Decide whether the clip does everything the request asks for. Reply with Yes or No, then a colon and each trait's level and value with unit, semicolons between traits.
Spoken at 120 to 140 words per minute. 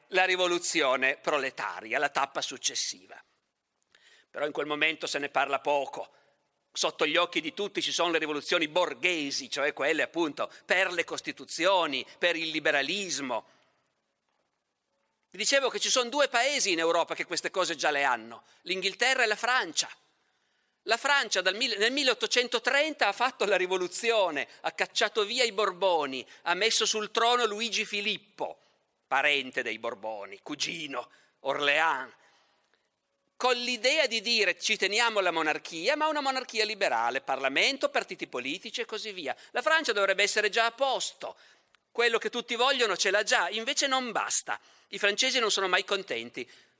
No: average, 155 wpm